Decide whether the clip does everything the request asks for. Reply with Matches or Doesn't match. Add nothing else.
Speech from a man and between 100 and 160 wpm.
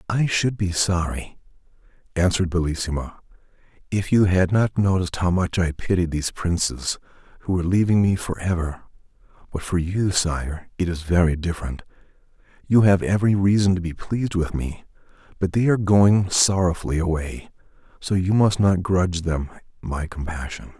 Matches